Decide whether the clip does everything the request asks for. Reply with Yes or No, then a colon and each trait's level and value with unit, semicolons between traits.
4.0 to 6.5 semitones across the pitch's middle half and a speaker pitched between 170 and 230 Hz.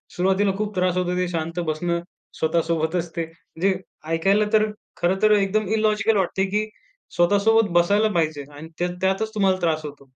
No: average, 3.6 semitones; medium, 185 Hz